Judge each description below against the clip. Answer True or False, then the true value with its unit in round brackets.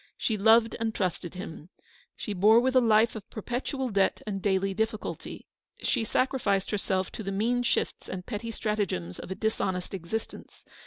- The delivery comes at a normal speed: True (170 wpm)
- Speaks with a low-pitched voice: False (210 Hz)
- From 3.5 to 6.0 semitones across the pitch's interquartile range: False (3.0 semitones)